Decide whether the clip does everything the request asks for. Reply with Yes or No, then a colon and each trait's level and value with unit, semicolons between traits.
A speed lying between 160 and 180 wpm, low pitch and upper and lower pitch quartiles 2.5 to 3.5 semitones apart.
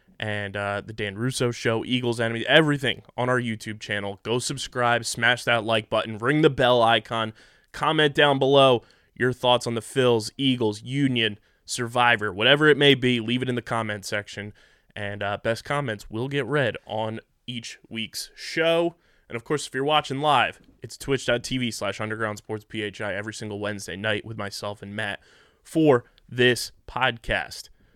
Yes: average, 170 wpm; low, 115 Hz; average, 3.1 semitones